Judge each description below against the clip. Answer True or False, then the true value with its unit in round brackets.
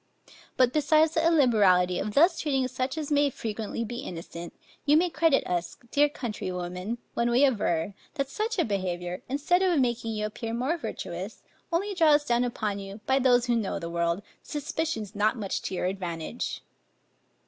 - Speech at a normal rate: True (170 wpm)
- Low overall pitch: False (240 Hz)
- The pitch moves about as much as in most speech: False (6.9 semitones)